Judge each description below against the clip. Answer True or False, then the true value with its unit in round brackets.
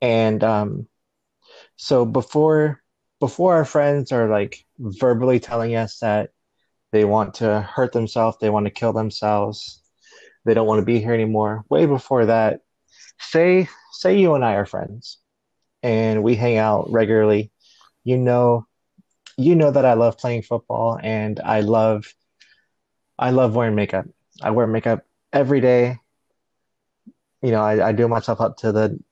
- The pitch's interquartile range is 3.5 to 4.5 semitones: False (2.7 semitones)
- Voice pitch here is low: True (115 Hz)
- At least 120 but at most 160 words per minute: True (155 wpm)